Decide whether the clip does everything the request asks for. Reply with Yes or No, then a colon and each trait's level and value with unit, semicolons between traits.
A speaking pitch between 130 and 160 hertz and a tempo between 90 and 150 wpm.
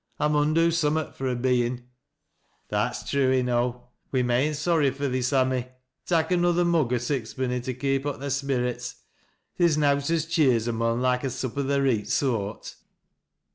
No: low, 135 Hz; average, 175 wpm